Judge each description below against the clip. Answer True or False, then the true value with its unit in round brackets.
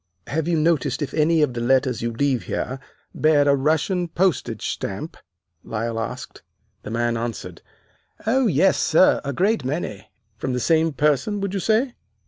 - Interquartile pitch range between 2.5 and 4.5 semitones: False (5.3 semitones)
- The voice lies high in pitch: False (150 Hz)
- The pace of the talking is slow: False (165 wpm)